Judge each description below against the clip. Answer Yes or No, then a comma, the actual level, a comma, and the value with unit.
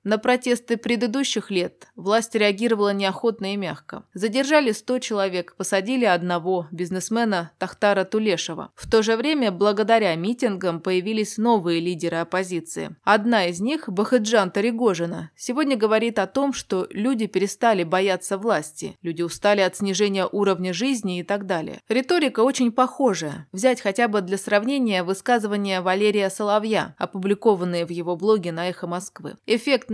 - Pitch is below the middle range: No, high, 205 Hz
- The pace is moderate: Yes, average, 140 wpm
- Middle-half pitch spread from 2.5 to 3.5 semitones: No, average, 3.9 semitones